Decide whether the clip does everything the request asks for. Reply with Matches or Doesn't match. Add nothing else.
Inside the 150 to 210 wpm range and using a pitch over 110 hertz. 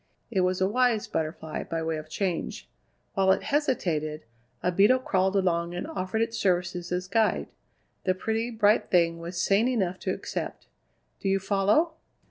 Matches